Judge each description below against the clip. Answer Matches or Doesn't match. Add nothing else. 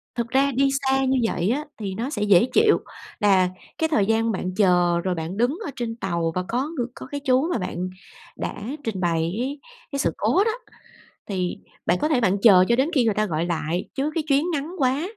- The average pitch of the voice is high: Matches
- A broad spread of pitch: Matches